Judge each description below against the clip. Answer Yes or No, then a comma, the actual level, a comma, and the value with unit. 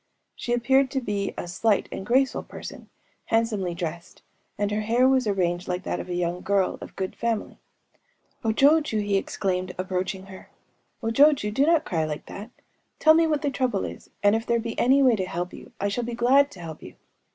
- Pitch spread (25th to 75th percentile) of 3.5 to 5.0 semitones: No, wide, 5.4 semitones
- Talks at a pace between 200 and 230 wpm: Yes, fast, 205 wpm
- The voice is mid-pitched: No, high, 215 Hz